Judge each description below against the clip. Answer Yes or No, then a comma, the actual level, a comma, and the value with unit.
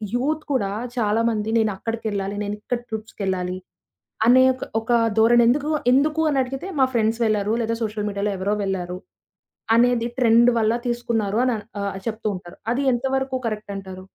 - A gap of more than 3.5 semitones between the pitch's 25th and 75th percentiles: No, average, 3.2 semitones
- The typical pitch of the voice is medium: No, high, 225 Hz